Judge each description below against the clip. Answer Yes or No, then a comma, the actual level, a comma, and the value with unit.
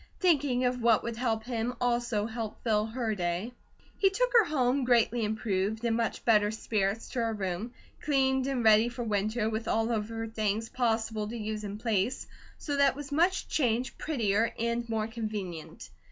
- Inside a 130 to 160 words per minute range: No, average, 180 wpm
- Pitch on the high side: Yes, high, 225 Hz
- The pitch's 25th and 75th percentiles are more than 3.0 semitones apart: No, narrow, 2.5 semitones